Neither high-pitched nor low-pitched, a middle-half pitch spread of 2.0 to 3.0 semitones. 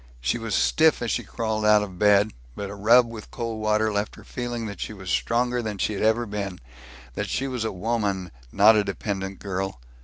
No: low, 105 Hz; narrow, 2.6 semitones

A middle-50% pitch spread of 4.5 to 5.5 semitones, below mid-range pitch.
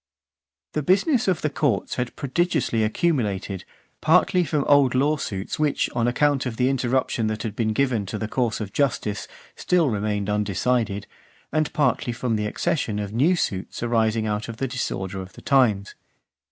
Yes: average, 5.2 semitones; low, 120 Hz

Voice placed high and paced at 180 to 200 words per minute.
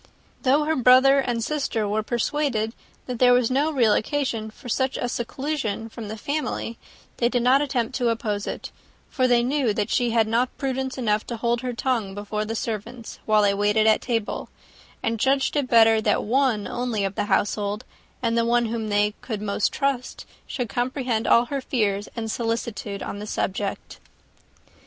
Yes: high, 235 Hz; average, 185 wpm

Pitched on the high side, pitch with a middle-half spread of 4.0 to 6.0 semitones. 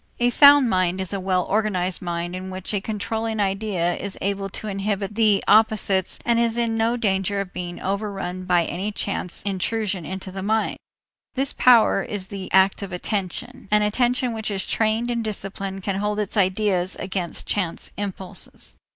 No: high, 200 Hz; narrow, 2.6 semitones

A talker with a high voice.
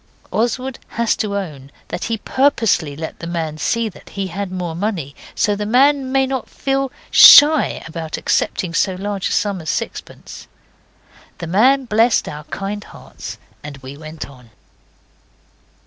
Yes: high, 200 Hz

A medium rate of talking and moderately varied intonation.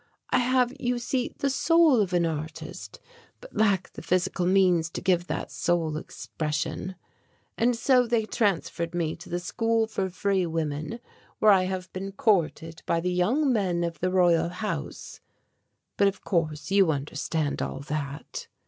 Yes: average, 160 wpm; average, 4.7 semitones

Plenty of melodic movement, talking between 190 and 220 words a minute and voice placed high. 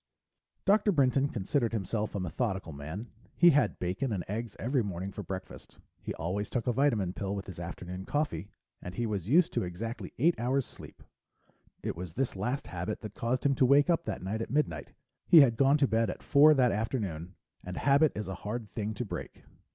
No: wide, 6.2 semitones; fast, 205 wpm; low, 110 Hz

